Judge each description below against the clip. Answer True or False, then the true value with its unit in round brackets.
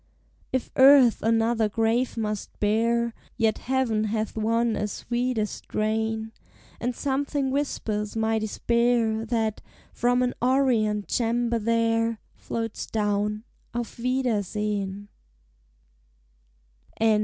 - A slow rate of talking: True (95 wpm)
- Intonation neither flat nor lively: False (2.0 semitones)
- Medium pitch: False (225 Hz)